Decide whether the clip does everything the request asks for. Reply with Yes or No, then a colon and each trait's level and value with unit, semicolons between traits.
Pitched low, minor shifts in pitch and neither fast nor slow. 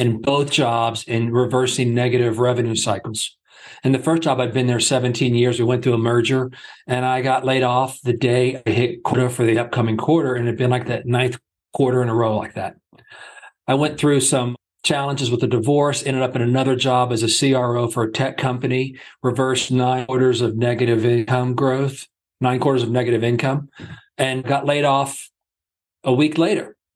Yes: low, 125 Hz; narrow, 1.8 semitones; average, 195 wpm